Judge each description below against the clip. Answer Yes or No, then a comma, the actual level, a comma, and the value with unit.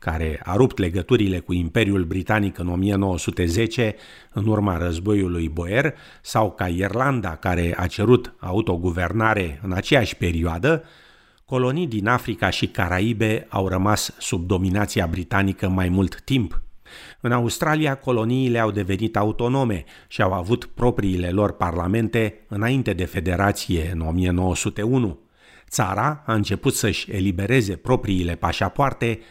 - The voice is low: Yes, low, 100 Hz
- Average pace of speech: Yes, average, 125 wpm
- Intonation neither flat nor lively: Yes, average, 4.2 semitones